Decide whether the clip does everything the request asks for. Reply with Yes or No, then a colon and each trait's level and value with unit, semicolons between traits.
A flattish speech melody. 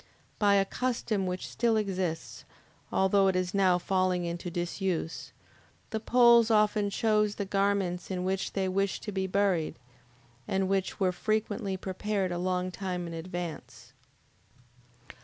Yes: narrow, 2.2 semitones